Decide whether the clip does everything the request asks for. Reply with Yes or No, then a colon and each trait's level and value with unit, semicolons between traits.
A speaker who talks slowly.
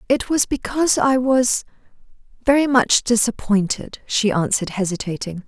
Yes: slow, 110 wpm